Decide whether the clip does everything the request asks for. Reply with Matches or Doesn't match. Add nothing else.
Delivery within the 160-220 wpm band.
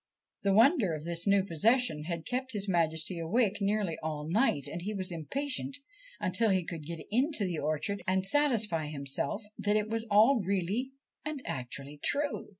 Matches